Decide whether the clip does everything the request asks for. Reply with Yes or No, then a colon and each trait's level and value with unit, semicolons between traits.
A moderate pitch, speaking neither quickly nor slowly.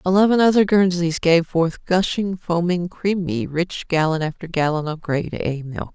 Yes: medium, 170 Hz; average, 160 wpm